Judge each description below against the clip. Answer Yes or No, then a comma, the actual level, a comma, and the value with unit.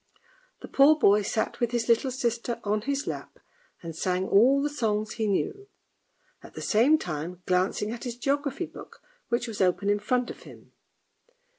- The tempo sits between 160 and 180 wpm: Yes, average, 175 wpm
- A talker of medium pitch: No, high, 230 Hz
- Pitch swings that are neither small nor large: Yes, average, 4.4 semitones